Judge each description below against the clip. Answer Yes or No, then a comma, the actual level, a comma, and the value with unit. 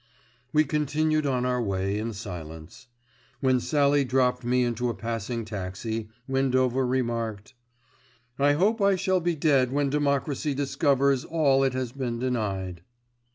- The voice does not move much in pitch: No, average, 3.6 semitones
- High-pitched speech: No, low, 130 Hz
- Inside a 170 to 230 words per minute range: No, average, 140 wpm